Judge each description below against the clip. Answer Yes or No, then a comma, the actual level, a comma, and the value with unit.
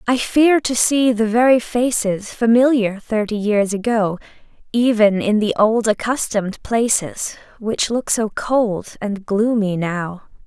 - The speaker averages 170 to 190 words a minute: No, average, 140 wpm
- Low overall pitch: No, high, 220 Hz